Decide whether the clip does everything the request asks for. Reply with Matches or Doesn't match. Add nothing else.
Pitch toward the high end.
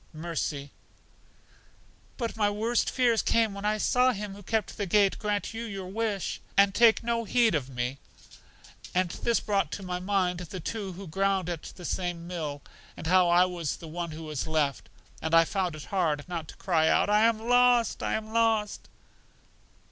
Matches